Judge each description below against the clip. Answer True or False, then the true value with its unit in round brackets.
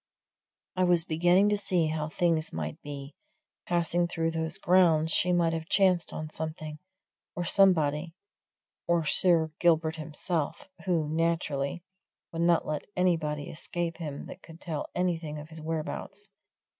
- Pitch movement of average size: False (2.1 semitones)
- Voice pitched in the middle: True (165 Hz)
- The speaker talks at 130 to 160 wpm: True (145 wpm)